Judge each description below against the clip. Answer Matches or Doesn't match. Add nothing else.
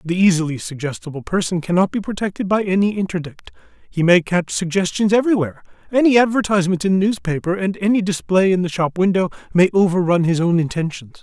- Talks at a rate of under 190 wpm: Matches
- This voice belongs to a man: Matches